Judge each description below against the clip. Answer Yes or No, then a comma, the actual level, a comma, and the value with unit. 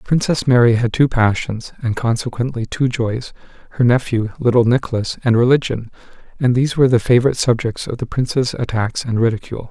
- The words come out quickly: No, average, 155 wpm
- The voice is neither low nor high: No, low, 120 Hz